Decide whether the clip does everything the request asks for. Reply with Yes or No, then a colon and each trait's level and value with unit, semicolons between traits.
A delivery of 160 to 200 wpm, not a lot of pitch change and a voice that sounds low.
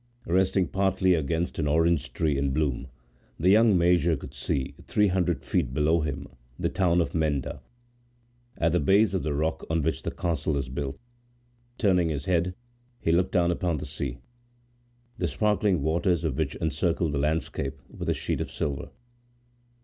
No: average, 170 wpm; average, 3.6 semitones; very low, 80 Hz